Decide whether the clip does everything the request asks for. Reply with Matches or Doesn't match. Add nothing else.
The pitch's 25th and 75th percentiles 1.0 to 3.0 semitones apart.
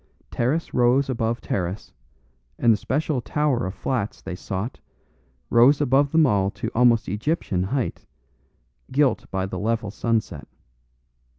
Doesn't match